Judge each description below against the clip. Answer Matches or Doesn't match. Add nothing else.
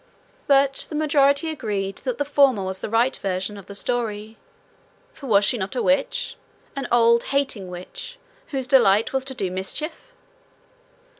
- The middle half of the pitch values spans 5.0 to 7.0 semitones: Matches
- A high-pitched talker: Matches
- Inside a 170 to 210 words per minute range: Doesn't match